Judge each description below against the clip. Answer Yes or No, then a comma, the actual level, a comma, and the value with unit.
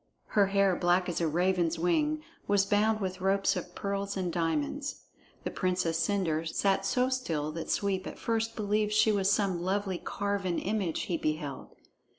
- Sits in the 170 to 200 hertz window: Yes, high, 190 Hz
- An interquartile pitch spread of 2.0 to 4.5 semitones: Yes, average, 2.9 semitones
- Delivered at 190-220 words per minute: No, average, 165 wpm